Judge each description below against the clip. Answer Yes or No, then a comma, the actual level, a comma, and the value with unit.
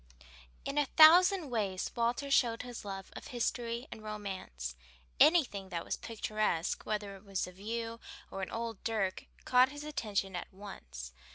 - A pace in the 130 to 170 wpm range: Yes, average, 160 wpm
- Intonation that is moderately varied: Yes, average, 4.2 semitones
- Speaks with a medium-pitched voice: No, high, 215 Hz